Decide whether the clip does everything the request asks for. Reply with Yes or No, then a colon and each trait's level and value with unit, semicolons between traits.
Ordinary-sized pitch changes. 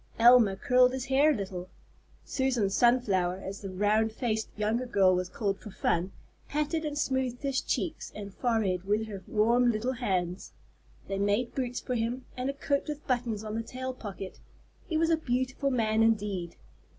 Yes: average, 4.3 semitones